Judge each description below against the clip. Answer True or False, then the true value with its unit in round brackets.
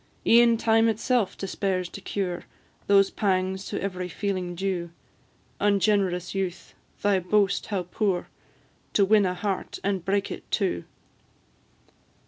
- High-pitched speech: True (195 Hz)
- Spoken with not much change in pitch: True (1.9 semitones)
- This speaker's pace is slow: True (125 wpm)